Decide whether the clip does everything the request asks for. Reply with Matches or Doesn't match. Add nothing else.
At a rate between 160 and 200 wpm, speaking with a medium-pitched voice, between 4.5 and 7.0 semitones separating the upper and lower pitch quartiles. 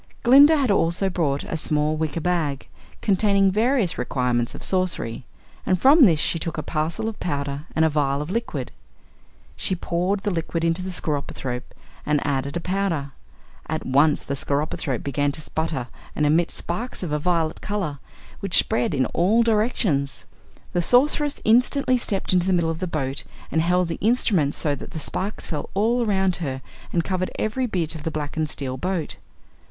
Matches